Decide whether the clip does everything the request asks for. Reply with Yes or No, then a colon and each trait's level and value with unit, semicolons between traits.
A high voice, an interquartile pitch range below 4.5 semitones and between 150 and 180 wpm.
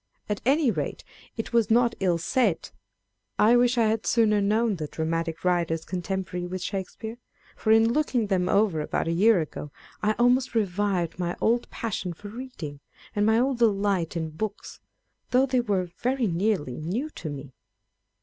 No: high, 205 Hz; average, 5.0 semitones; average, 170 wpm